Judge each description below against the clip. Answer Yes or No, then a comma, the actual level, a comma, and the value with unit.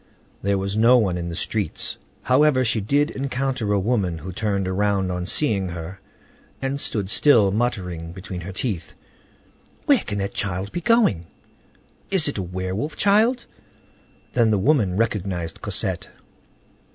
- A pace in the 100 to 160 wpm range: Yes, average, 150 wpm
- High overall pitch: No, low, 100 Hz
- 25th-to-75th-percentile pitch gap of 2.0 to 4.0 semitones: No, wide, 5.5 semitones